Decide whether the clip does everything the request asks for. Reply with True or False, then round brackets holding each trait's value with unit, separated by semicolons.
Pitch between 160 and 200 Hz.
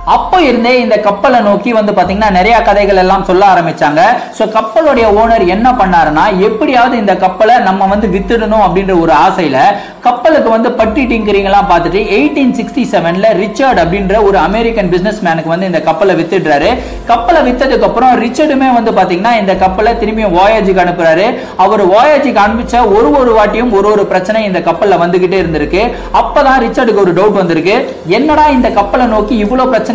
False (215 Hz)